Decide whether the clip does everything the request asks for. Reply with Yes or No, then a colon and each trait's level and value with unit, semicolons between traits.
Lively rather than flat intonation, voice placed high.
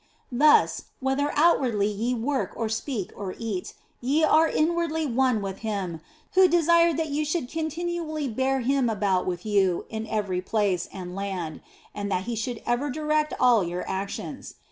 Yes: wide, 7.2 semitones; high, 240 Hz